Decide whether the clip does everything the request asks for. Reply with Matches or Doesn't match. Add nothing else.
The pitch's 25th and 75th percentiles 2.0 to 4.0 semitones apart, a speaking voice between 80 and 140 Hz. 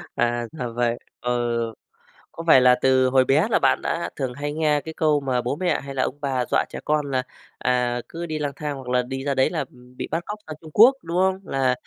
Matches